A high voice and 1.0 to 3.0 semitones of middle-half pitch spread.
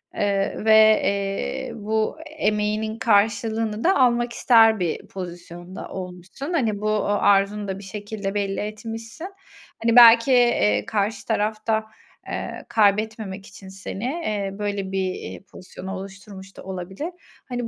Yes: high, 210 Hz; narrow, 2.5 semitones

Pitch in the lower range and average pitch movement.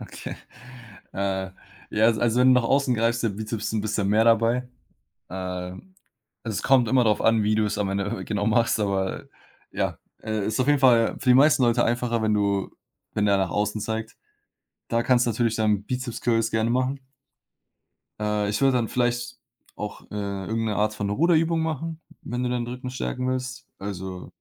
Yes: low, 115 Hz; average, 3.1 semitones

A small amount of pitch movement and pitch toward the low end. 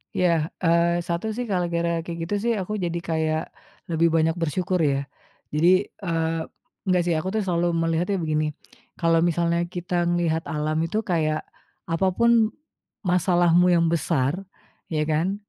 No: narrow, 1.8 semitones; medium, 170 Hz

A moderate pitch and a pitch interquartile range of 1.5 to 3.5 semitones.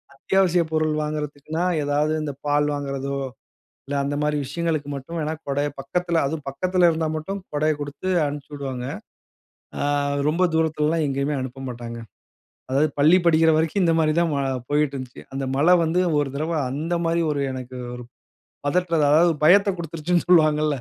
Yes: medium, 150 Hz; average, 2.7 semitones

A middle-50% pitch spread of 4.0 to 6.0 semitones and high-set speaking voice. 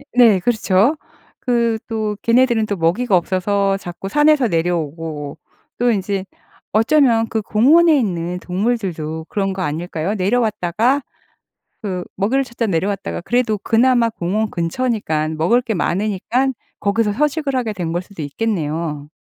Yes: average, 5.2 semitones; high, 205 Hz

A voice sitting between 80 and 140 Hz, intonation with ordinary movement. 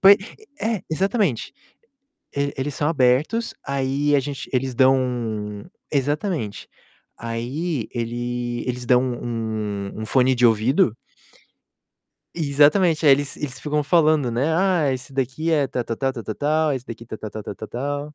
Yes: low, 135 Hz; average, 3.9 semitones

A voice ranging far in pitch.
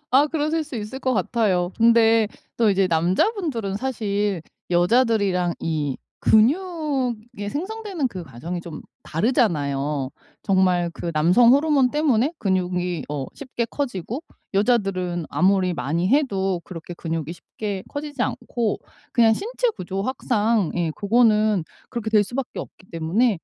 Yes: wide, 6.1 semitones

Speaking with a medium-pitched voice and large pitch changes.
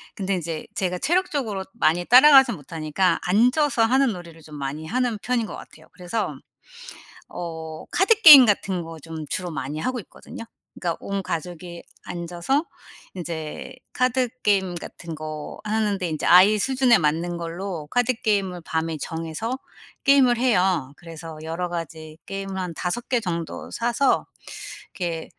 Yes: medium, 180 Hz; wide, 6.1 semitones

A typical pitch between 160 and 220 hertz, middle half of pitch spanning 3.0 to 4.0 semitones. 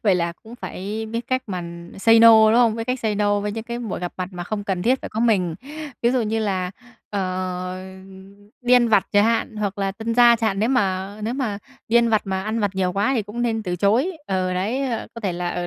Yes: high, 210 Hz; average, 3.4 semitones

